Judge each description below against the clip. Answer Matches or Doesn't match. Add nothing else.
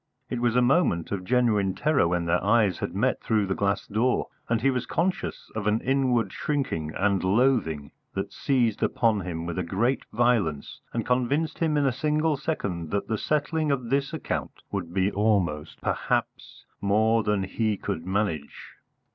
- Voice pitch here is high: Doesn't match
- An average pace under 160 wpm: Doesn't match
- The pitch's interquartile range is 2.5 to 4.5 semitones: Doesn't match